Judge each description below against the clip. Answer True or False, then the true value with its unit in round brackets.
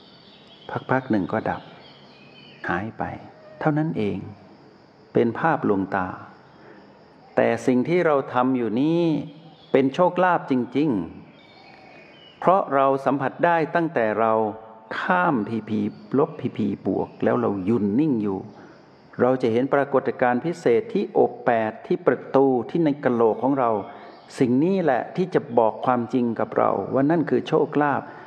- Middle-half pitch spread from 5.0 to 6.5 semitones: True (5.6 semitones)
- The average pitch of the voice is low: True (130 Hz)